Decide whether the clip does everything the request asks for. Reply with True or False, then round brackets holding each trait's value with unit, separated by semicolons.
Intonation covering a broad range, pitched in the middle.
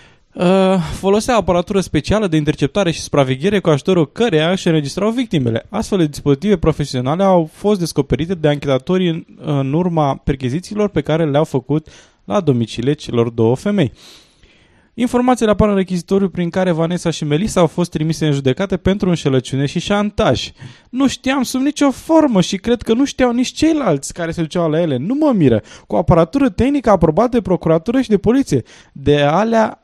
True (5.7 semitones; 180 Hz)